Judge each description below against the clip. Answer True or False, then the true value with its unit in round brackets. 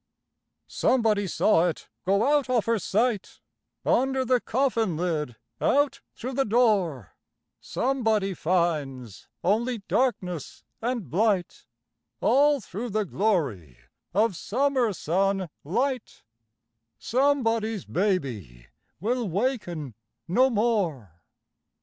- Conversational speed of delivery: False (95 wpm)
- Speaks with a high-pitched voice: True (210 Hz)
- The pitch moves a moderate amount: False (6.3 semitones)